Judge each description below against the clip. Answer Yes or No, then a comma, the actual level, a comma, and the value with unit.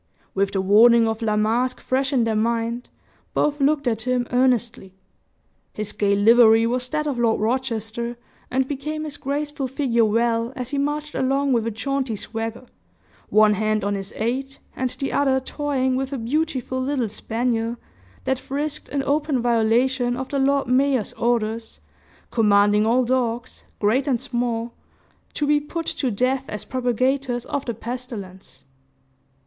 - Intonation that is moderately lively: Yes, average, 3.1 semitones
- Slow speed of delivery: No, average, 155 wpm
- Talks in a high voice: Yes, high, 245 Hz